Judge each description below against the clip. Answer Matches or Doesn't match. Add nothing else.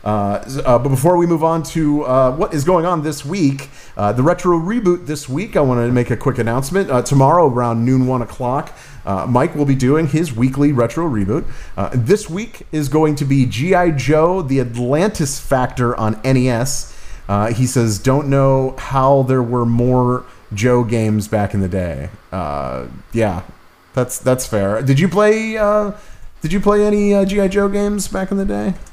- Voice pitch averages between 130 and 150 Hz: Matches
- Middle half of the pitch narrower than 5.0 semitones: Doesn't match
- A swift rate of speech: Doesn't match